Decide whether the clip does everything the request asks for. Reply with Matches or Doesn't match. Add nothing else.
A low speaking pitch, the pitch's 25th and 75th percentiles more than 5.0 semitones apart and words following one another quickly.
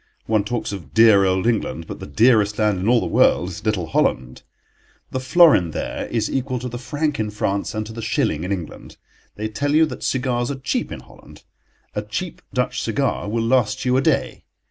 Doesn't match